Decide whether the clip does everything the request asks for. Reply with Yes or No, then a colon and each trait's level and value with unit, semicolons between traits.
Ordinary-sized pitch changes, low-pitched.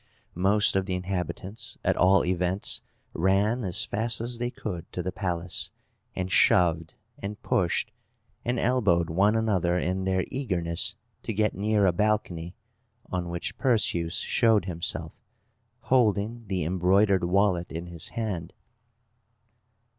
Yes: average, 3.5 semitones; very low, 95 Hz